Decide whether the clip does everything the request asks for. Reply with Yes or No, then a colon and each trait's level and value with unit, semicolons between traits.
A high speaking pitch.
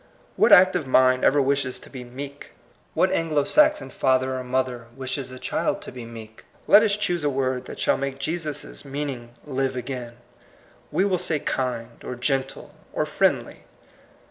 No: low, 135 Hz